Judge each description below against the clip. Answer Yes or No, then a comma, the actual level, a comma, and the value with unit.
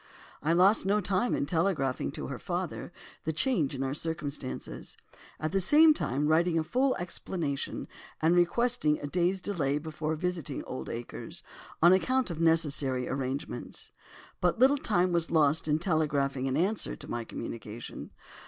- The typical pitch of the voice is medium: Yes, medium, 160 Hz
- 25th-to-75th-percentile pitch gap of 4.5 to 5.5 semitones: Yes, average, 4.8 semitones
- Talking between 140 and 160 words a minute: Yes, average, 155 wpm